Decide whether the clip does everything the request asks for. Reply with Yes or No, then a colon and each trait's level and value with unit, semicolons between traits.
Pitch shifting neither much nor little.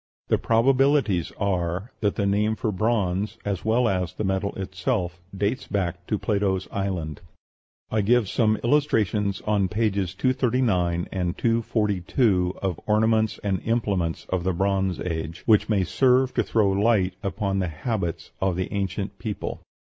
Yes: average, 3.2 semitones